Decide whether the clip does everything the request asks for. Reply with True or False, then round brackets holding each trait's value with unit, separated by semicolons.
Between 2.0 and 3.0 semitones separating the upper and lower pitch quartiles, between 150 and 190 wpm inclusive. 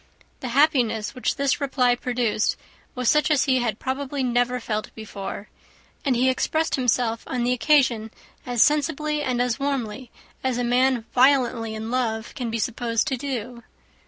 True (2.6 semitones; 160 wpm)